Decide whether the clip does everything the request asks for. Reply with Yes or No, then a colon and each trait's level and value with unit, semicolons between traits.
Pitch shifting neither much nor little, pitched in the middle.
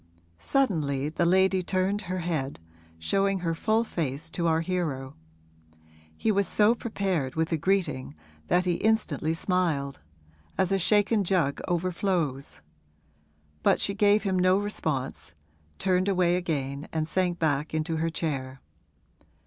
Yes: average, 4.1 semitones; medium, 175 Hz